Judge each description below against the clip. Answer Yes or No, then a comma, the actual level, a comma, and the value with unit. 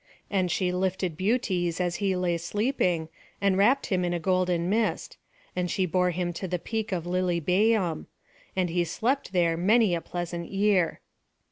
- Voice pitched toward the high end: No, medium, 180 Hz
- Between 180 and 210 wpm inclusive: No, average, 165 wpm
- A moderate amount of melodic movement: No, narrow, 2.3 semitones